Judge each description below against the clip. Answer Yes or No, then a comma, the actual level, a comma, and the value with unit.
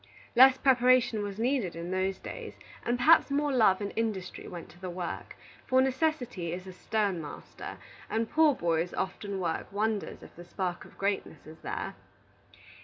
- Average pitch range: No, wide, 6.0 semitones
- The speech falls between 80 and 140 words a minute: No, average, 170 wpm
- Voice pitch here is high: Yes, high, 205 Hz